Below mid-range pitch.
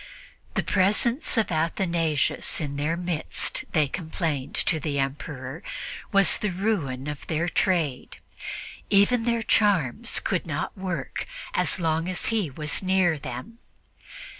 No: medium, 170 Hz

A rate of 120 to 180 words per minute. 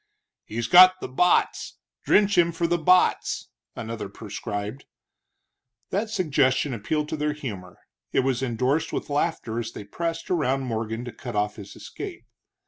Yes: average, 150 wpm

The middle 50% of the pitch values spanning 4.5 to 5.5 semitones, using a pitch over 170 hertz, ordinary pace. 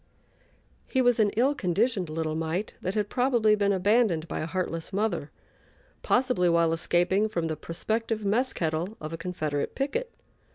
Yes: average, 5.2 semitones; high, 190 Hz; average, 160 wpm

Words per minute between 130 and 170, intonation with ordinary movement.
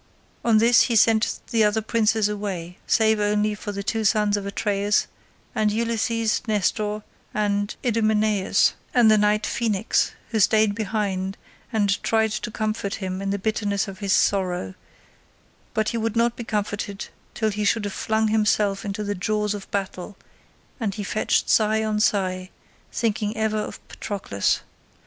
No: average, 155 wpm; narrow, 1.5 semitones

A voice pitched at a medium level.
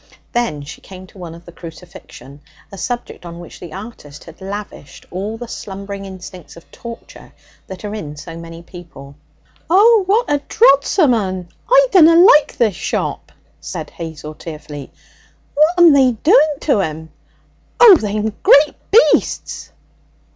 No: high, 195 Hz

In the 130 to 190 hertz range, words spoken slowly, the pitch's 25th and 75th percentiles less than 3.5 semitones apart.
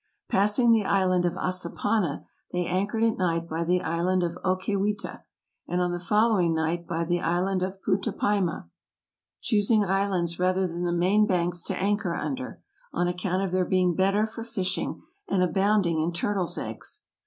No: medium, 185 Hz; average, 165 wpm; narrow, 2.6 semitones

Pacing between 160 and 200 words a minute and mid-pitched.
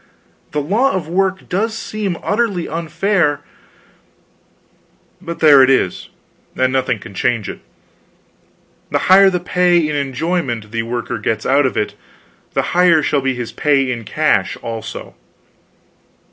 No: average, 140 wpm; medium, 150 Hz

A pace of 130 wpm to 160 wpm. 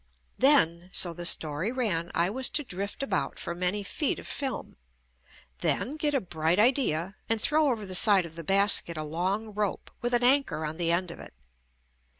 No: average, 190 wpm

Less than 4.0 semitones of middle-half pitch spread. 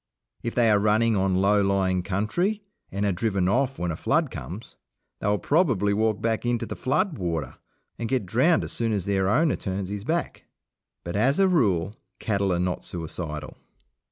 No: average, 4.3 semitones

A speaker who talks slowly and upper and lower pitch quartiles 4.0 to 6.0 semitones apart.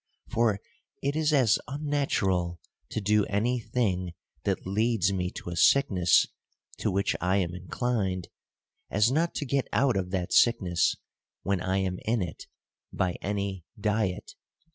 No: average, 145 wpm; average, 4.6 semitones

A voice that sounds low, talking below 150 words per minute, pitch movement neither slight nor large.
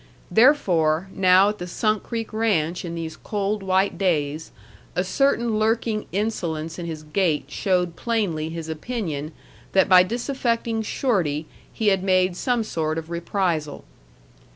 No: medium, 185 Hz; average, 140 wpm; average, 5.0 semitones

